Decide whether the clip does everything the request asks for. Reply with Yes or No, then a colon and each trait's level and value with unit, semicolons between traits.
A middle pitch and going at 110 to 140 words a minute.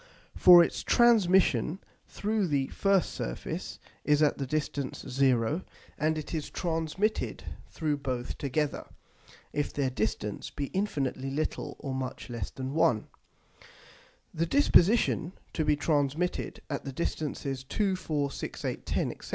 Yes: medium, 150 Hz; slow, 135 wpm